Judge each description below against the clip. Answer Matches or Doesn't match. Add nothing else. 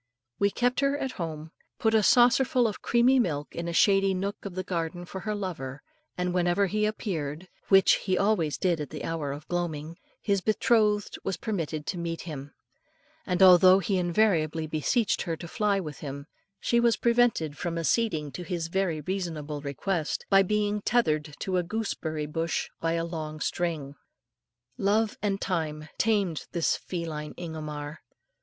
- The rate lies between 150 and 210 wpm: Matches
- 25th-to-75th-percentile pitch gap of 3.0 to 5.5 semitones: Matches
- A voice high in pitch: Doesn't match